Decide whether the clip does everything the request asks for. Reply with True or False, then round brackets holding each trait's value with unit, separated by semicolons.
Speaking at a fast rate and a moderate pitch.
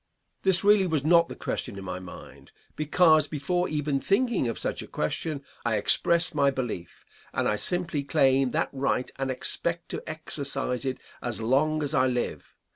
False (175 wpm; 145 Hz)